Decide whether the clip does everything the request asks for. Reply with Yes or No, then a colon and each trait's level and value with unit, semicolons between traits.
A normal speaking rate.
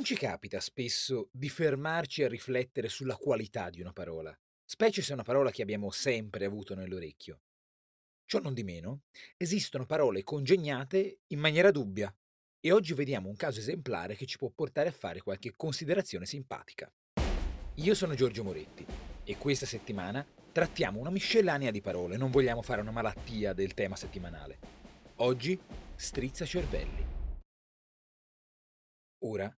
Yes: average, 145 wpm